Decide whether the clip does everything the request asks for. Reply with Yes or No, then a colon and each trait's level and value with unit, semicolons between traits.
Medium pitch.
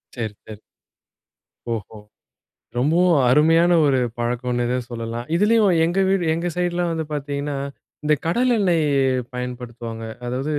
Yes: medium, 145 Hz